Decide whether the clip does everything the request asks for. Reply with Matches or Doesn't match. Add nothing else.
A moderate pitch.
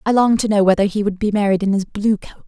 Doesn't match